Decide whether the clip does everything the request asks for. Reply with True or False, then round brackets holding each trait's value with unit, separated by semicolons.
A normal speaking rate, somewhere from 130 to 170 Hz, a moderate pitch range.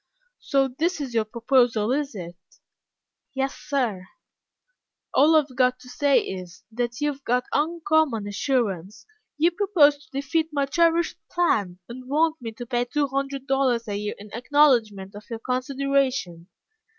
False (155 wpm; 260 Hz; 4.3 semitones)